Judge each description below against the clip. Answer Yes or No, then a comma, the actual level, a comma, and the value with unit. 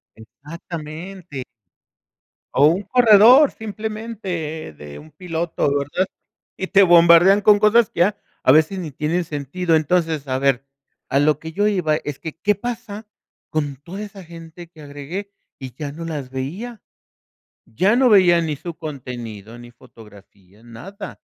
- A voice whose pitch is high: No, medium, 165 Hz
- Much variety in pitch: Yes, wide, 5.7 semitones